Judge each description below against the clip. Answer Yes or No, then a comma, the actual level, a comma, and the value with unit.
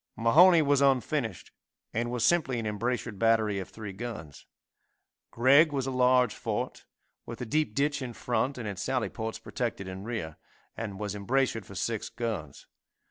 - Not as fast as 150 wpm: No, average, 165 wpm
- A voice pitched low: Yes, low, 115 Hz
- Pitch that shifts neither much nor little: Yes, average, 3.9 semitones